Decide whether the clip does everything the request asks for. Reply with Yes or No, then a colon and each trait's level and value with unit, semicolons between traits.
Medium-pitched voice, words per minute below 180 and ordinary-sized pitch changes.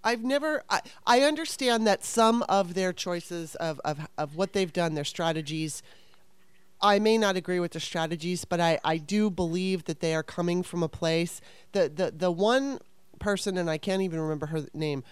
No: medium, 180 Hz; average, 195 wpm; average, 3.9 semitones